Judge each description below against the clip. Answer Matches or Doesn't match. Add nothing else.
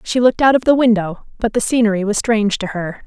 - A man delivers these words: Doesn't match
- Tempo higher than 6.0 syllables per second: Matches